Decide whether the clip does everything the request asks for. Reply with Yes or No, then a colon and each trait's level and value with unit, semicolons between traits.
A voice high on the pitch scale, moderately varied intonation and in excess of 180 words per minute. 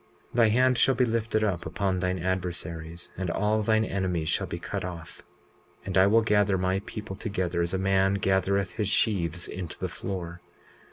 No: very low, 95 Hz; average, 3.1 semitones; average, 190 wpm